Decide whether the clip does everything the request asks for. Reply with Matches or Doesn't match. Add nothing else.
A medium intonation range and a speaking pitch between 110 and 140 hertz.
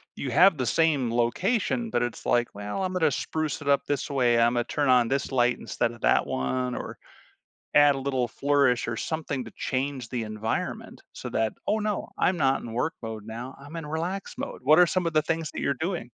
Matches